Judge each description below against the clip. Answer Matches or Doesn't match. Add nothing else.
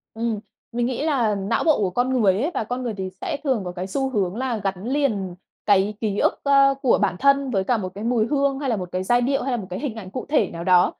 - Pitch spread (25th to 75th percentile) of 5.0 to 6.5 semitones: Matches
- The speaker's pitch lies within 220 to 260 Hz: Matches